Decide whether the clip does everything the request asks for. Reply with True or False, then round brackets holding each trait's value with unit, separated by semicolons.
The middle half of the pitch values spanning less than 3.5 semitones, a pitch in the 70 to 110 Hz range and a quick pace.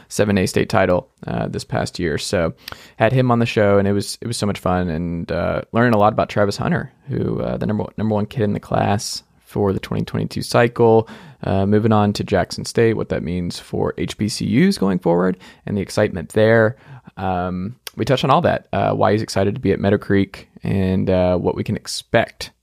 True (2.7 semitones; 100 Hz; 220 wpm)